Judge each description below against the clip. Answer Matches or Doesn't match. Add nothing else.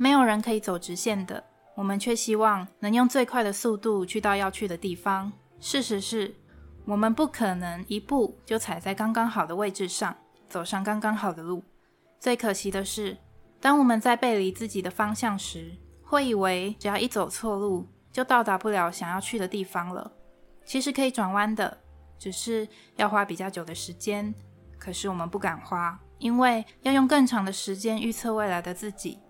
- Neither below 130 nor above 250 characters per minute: Doesn't match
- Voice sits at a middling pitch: Doesn't match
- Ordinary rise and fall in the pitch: Matches